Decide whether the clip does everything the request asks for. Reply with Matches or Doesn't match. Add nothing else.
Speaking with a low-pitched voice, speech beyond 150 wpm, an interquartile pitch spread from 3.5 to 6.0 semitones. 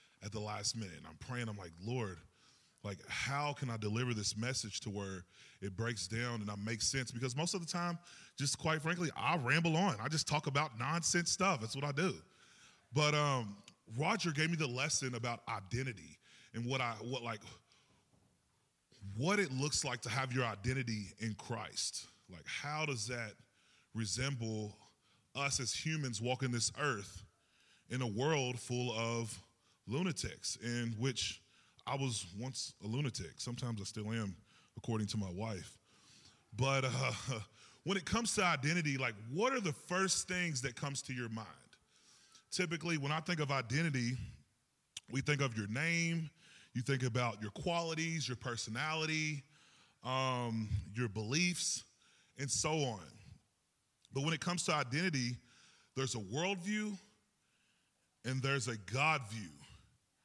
Matches